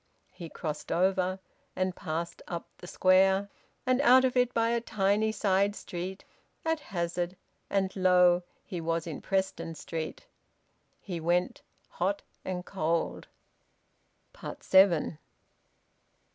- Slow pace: Yes, slow, 115 wpm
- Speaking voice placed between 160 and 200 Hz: Yes, medium, 185 Hz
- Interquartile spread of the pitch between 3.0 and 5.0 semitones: No, narrow, 2.6 semitones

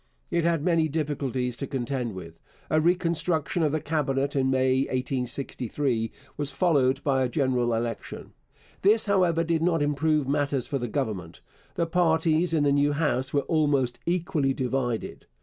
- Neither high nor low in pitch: Yes, medium, 145 Hz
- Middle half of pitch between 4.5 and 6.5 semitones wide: No, average, 3.8 semitones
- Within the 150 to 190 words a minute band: Yes, average, 155 wpm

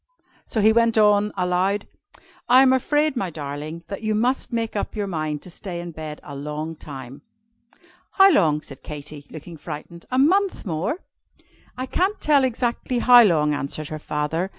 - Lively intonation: Yes, wide, 7.9 semitones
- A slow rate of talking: No, average, 175 wpm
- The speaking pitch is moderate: Yes, medium, 180 Hz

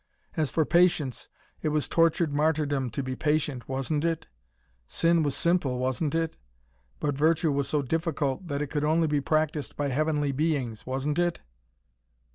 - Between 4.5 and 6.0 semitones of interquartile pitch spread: No, narrow, 2.6 semitones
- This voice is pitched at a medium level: Yes, medium, 150 Hz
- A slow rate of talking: No, average, 160 wpm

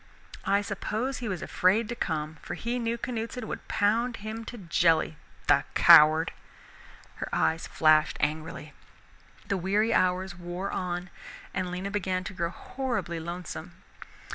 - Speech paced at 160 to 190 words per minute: No, average, 140 wpm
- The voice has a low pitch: No, medium, 185 Hz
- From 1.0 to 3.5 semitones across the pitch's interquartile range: No, average, 4.6 semitones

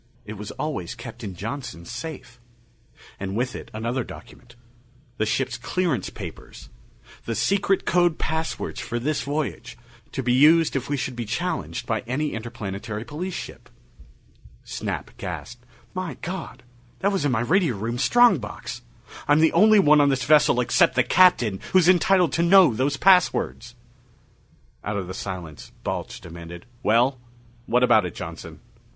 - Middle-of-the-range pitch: No, low, 130 Hz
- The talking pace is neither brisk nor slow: Yes, average, 155 wpm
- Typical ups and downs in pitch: No, wide, 6.4 semitones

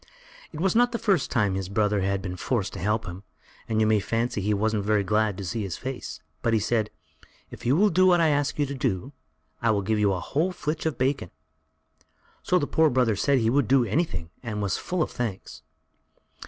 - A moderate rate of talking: No, fast, 220 wpm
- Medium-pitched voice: No, low, 115 Hz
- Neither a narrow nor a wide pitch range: No, wide, 5.9 semitones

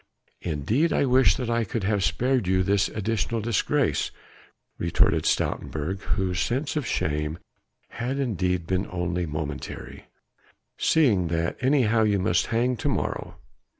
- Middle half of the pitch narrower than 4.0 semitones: No, average, 5.3 semitones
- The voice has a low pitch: Yes, low, 100 Hz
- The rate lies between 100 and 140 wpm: Yes, slow, 135 wpm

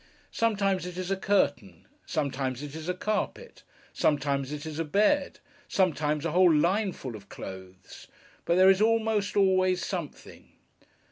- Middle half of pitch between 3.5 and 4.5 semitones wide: No, wide, 5.4 semitones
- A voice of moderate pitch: Yes, medium, 175 Hz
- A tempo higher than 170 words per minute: No, average, 150 wpm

